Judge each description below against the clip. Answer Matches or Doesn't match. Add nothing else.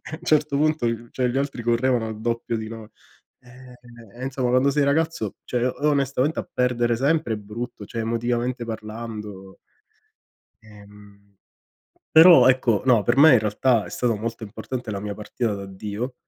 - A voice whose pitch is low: Matches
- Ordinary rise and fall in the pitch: Matches